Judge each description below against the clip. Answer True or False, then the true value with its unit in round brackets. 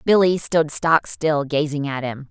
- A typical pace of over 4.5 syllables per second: False (4.1 syllables/s)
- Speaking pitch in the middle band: True (150 Hz)